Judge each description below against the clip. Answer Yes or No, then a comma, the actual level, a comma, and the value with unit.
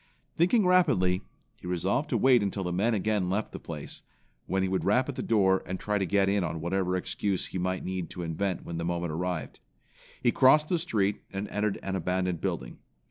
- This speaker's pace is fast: Yes, fast, 210 wpm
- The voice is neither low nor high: No, very low, 95 Hz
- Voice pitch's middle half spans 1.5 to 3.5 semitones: Yes, average, 2.9 semitones